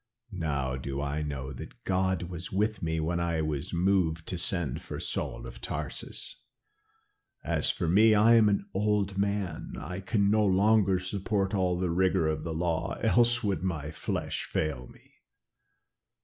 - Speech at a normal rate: Yes, average, 165 wpm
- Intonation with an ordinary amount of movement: Yes, average, 4.0 semitones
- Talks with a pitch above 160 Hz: No, very low, 90 Hz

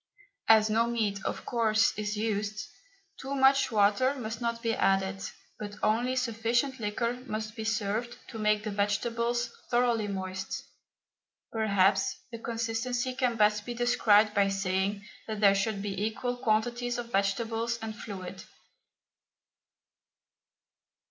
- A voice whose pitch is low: No, high, 220 Hz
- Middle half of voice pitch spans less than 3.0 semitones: Yes, narrow, 2.5 semitones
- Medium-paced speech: No, slow, 130 wpm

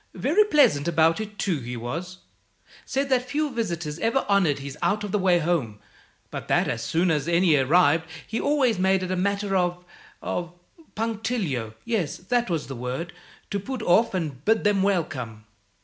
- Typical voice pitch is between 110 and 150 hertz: No, medium, 180 Hz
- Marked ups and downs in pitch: Yes, wide, 5.9 semitones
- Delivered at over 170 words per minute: Yes, average, 180 wpm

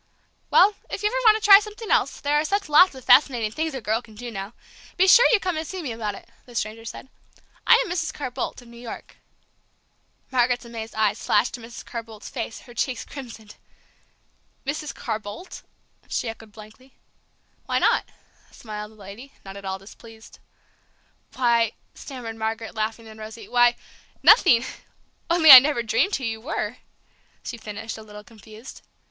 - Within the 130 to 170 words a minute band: No, average, 180 wpm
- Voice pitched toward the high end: Yes, high, 235 Hz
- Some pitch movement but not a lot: Yes, average, 4.7 semitones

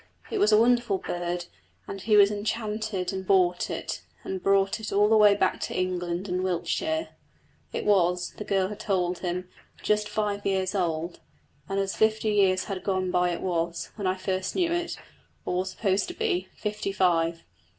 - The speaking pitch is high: Yes, high, 195 Hz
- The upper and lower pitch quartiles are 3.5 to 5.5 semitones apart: No, narrow, 2.6 semitones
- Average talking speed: Yes, average, 185 wpm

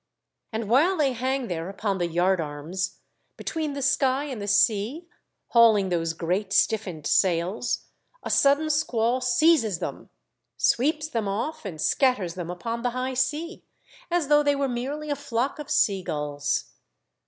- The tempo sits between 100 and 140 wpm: No, average, 155 wpm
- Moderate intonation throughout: No, wide, 6.9 semitones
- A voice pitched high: Yes, high, 235 Hz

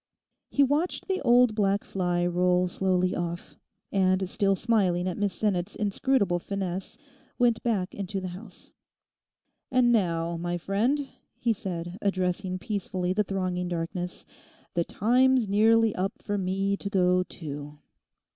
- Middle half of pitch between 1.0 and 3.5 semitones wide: Yes, average, 3.0 semitones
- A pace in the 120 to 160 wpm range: Yes, slow, 135 wpm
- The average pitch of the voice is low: No, high, 190 Hz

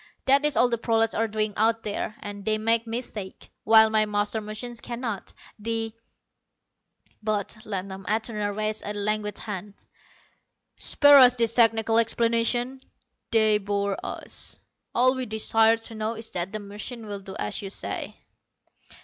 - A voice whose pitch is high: Yes, high, 220 Hz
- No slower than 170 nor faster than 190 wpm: No, average, 155 wpm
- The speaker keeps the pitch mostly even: Yes, narrow, 1.8 semitones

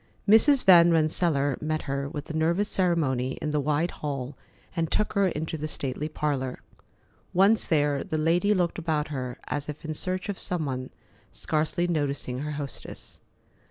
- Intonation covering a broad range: No, average, 3.3 semitones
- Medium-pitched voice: Yes, medium, 155 Hz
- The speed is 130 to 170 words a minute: Yes, average, 160 wpm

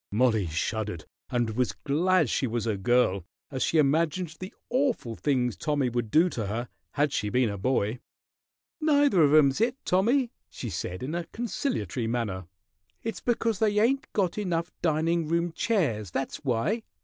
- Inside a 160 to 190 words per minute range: Yes, average, 165 wpm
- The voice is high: No, medium, 145 Hz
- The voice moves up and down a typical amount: No, wide, 8.2 semitones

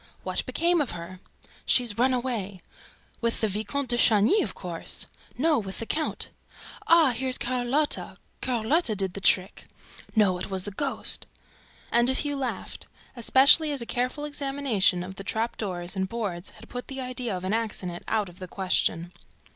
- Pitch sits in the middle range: No, high, 230 Hz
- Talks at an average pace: Yes, average, 170 wpm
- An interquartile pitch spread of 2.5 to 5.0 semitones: No, wide, 5.5 semitones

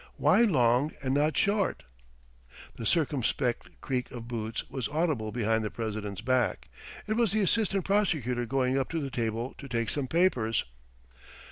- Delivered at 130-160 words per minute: Yes, average, 155 wpm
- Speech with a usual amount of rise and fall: No, wide, 5.8 semitones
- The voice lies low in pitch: Yes, low, 130 Hz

